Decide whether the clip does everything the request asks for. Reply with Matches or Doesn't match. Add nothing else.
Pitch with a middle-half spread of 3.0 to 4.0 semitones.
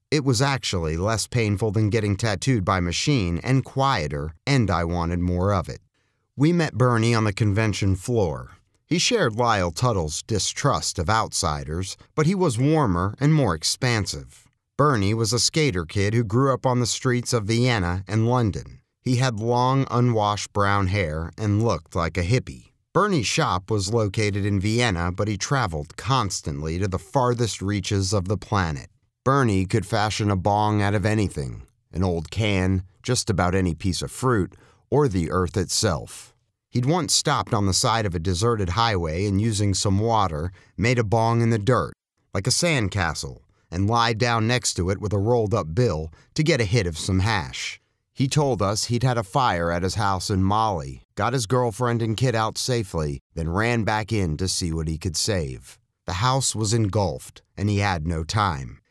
Doesn't match